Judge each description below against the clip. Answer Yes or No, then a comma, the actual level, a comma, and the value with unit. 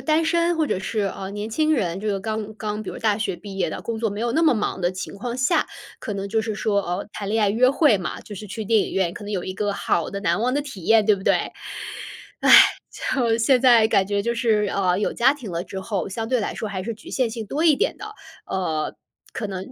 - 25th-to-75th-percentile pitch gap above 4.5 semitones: No, average, 3.2 semitones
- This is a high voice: Yes, high, 215 Hz